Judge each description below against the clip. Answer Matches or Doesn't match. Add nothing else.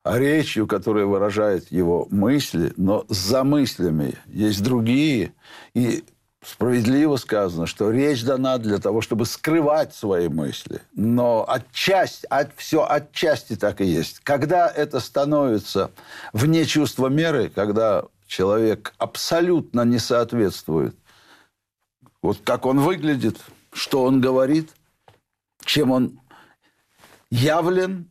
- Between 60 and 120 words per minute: Matches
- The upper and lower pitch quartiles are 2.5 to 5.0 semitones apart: Doesn't match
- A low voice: Matches